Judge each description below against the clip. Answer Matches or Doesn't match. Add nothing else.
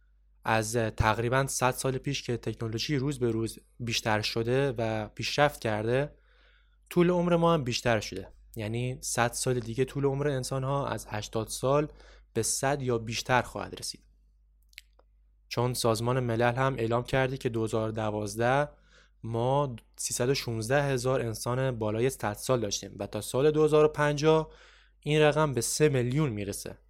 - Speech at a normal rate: Matches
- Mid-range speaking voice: Doesn't match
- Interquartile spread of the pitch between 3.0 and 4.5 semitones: Matches